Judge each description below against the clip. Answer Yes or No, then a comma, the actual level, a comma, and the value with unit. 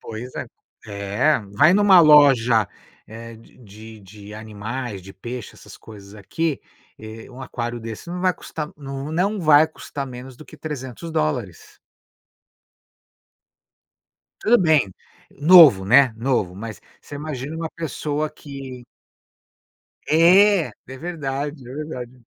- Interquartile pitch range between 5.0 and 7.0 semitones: Yes, wide, 5.6 semitones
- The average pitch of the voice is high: No, low, 130 Hz